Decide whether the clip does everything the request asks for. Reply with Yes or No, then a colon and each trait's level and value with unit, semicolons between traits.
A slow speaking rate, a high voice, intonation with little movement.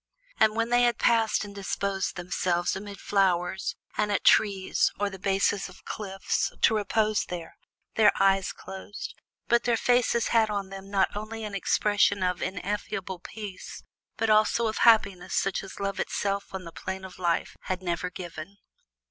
No: average, 170 wpm; high, 200 Hz; narrow, 2.2 semitones